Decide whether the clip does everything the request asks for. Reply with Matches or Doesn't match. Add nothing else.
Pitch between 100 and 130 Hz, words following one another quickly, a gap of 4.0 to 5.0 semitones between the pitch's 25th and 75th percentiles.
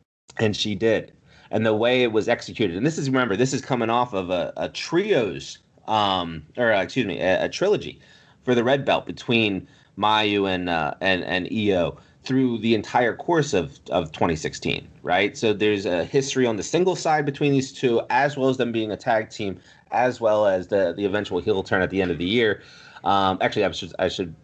Matches